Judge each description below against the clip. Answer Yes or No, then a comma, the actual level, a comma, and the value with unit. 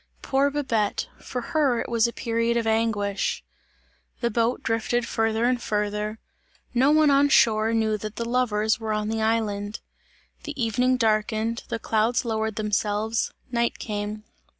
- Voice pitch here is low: No, high, 225 Hz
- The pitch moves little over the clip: Yes, narrow, 1.9 semitones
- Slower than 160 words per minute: Yes, average, 150 wpm